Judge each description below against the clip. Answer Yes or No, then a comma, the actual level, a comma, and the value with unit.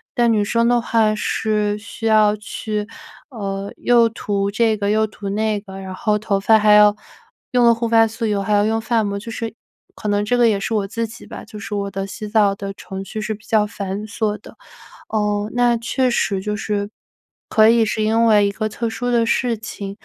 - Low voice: No, high, 215 Hz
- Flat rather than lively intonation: Yes, narrow, 1.8 semitones